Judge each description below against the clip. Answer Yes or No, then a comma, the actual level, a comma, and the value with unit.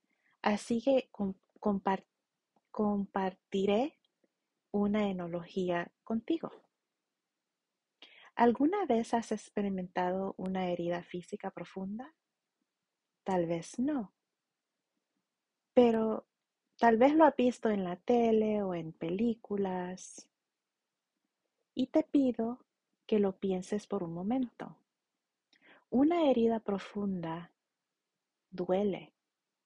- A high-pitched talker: Yes, high, 205 Hz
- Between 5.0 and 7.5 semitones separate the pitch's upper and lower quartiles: No, average, 4.4 semitones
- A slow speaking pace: Yes, slow, 85 wpm